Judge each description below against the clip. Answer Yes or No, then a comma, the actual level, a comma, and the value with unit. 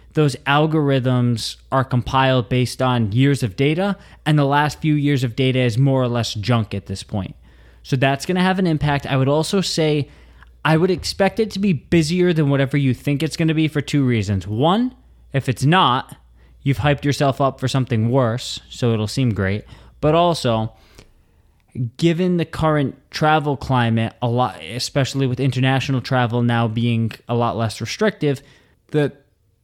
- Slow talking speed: No, average, 180 wpm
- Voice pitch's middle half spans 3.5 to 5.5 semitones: Yes, average, 4.4 semitones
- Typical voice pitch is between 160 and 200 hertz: No, low, 130 Hz